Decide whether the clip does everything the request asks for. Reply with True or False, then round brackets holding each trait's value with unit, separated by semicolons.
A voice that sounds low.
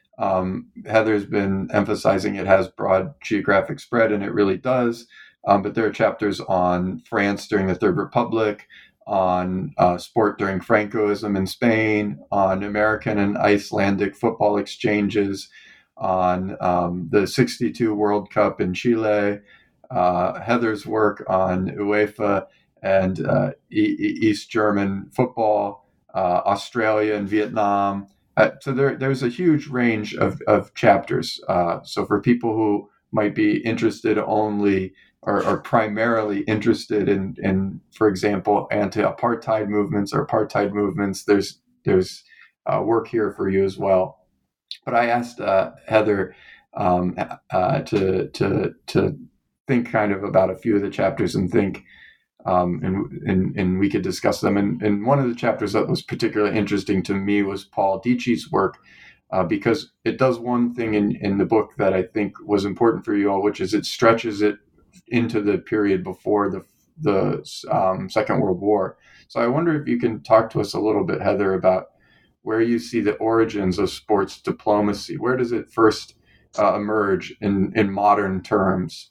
True (105 Hz)